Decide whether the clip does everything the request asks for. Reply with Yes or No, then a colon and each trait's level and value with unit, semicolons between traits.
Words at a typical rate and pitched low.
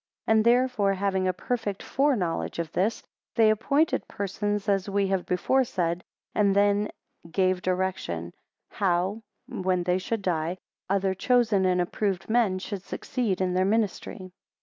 No: average, 155 wpm; high, 195 Hz